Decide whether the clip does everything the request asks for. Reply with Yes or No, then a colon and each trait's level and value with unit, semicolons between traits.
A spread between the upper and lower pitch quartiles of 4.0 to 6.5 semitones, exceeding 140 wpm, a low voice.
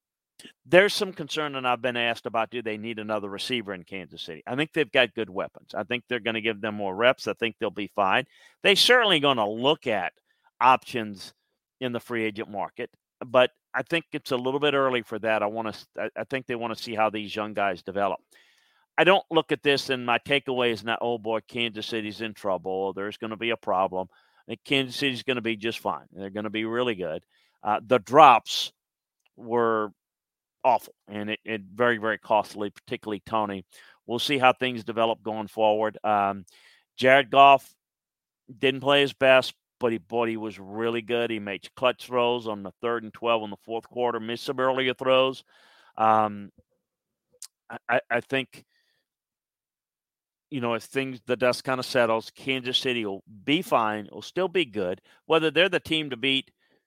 No: average, 3.4 semitones; average, 200 wpm; low, 120 Hz